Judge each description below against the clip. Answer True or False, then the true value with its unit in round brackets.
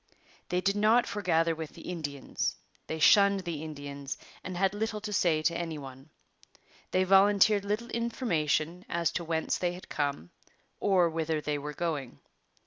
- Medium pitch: True (170 Hz)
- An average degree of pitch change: True (4.4 semitones)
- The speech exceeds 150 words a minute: True (160 wpm)